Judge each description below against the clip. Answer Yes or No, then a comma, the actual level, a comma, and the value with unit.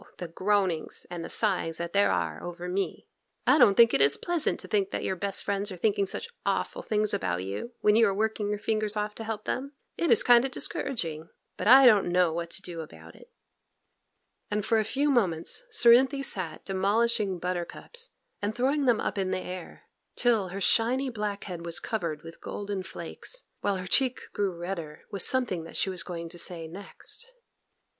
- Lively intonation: No, average, 4.7 semitones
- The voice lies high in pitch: Yes, high, 200 Hz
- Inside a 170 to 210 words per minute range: Yes, average, 200 wpm